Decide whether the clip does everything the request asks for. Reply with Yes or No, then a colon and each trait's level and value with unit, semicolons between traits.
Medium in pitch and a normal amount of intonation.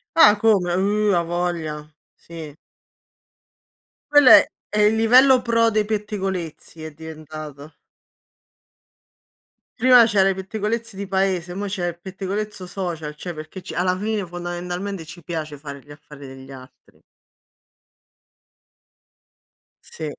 Yes: medium, 180 Hz; average, 4.8 semitones